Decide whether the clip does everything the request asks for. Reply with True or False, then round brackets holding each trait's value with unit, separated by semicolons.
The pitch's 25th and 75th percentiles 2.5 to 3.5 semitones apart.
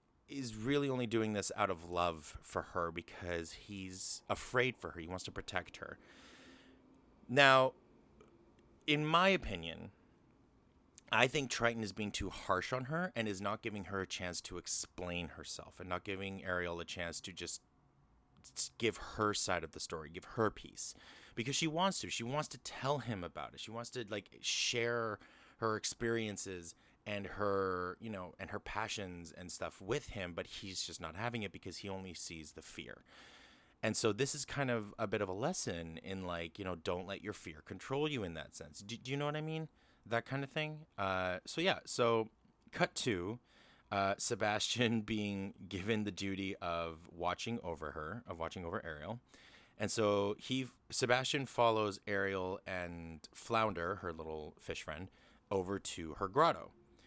False (4.8 semitones)